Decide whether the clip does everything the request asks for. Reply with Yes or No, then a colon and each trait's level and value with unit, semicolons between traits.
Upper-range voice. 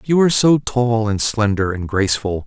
No: low, 115 Hz